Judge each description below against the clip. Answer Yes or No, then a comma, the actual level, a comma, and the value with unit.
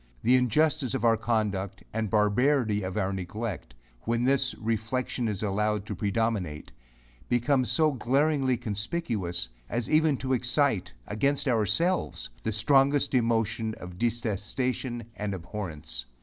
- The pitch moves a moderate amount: Yes, average, 3.7 semitones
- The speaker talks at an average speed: No, slow, 125 wpm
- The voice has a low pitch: Yes, low, 115 Hz